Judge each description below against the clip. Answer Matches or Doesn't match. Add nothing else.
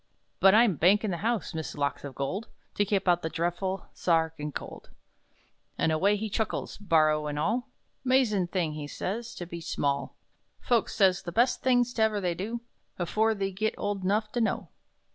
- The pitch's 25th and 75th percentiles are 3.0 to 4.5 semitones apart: Doesn't match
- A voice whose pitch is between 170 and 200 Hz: Matches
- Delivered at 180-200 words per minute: Matches